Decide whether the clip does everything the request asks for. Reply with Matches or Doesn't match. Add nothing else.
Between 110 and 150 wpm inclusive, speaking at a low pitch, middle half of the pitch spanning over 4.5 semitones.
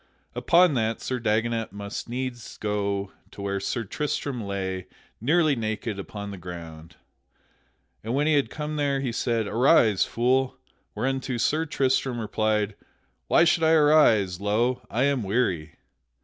Matches